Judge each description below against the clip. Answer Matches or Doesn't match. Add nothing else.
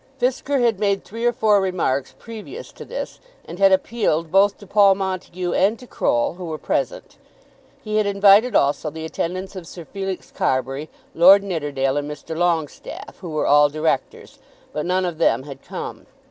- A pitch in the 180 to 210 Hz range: Matches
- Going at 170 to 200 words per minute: Matches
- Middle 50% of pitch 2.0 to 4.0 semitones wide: Doesn't match